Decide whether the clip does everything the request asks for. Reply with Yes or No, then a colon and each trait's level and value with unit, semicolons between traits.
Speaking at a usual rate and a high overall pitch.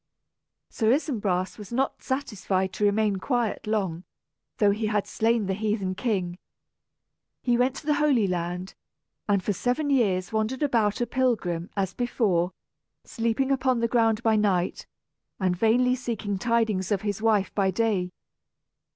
Yes: average, 150 wpm; high, 215 Hz